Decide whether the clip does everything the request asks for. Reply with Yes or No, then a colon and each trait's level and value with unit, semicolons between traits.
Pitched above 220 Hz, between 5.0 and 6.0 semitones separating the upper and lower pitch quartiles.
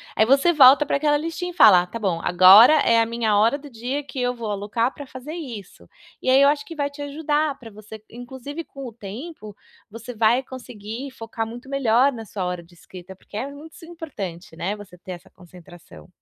Yes: high, 235 Hz; wide, 5.5 semitones